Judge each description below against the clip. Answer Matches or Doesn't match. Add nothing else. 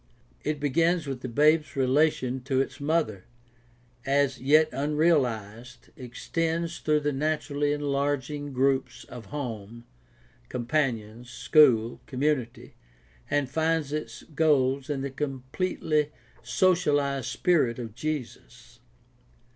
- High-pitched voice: Doesn't match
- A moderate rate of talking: Doesn't match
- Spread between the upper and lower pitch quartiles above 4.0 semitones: Doesn't match